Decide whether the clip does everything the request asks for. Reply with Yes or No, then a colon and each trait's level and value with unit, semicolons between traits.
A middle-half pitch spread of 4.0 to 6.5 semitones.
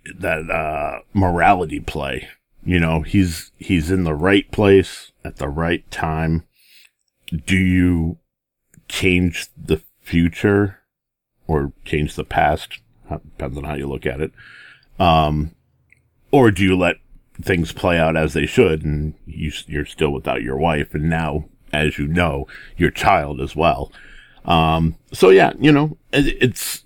No: average, 3.3 semitones